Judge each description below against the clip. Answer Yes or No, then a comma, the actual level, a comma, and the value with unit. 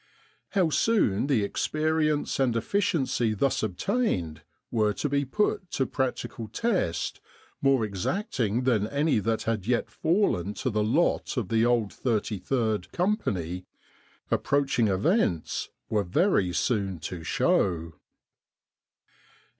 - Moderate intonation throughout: No, wide, 6.9 semitones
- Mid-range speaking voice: No, low, 115 Hz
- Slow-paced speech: Yes, slow, 115 wpm